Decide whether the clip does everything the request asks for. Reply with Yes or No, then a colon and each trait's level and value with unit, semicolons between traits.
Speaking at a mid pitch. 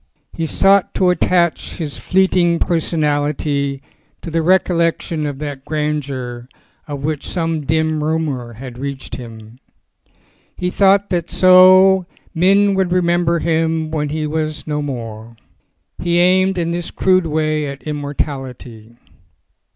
Yes: medium, 155 Hz